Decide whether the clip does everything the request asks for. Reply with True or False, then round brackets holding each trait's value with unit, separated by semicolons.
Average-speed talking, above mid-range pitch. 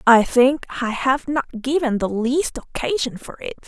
True (180 wpm; 260 Hz)